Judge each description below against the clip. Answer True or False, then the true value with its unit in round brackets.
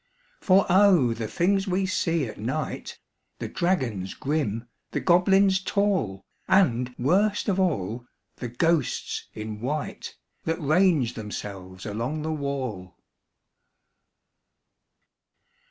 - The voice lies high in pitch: False (150 Hz)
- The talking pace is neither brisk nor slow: False (105 wpm)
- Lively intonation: True (8.5 semitones)